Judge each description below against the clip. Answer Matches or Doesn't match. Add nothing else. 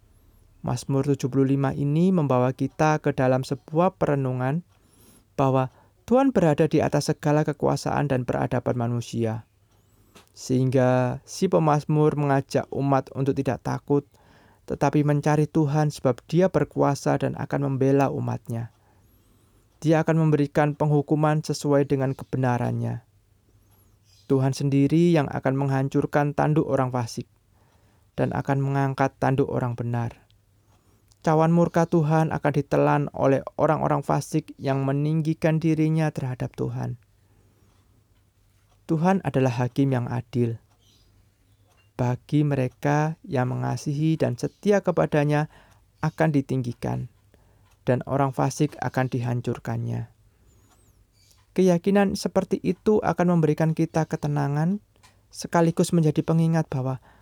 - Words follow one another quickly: Doesn't match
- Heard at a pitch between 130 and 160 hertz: Matches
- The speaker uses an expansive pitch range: Matches